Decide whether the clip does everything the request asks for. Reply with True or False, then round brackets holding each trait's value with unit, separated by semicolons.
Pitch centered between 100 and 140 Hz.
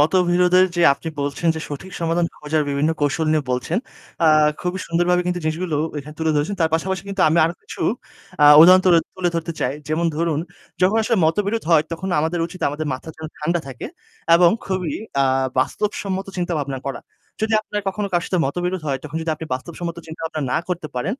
False (170 Hz)